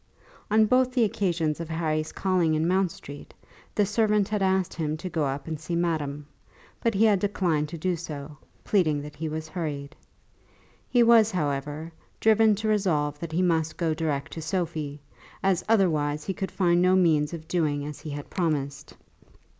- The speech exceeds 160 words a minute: Yes, average, 180 wpm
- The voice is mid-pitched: Yes, medium, 165 Hz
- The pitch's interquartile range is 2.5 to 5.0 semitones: Yes, average, 4.0 semitones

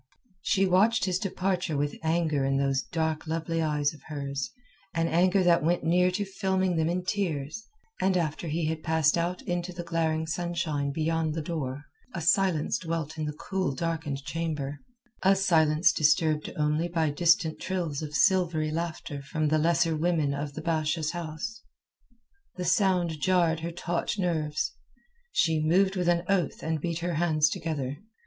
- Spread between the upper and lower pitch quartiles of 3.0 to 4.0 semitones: No, narrow, 2.5 semitones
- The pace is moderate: Yes, average, 165 wpm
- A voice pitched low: No, medium, 165 Hz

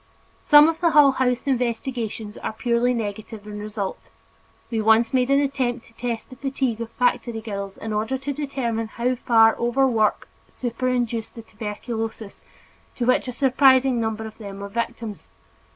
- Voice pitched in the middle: No, high, 235 Hz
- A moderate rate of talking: Yes, average, 165 wpm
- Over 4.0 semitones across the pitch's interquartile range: No, narrow, 2.6 semitones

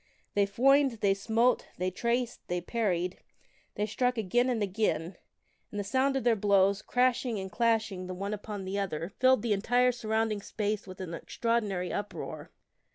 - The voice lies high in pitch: Yes, high, 210 Hz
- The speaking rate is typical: Yes, average, 170 wpm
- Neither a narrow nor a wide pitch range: Yes, average, 3.5 semitones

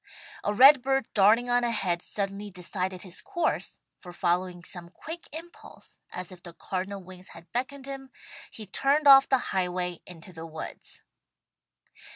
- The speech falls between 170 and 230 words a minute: No, average, 155 wpm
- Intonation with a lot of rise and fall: Yes, wide, 6.8 semitones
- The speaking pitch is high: Yes, high, 195 Hz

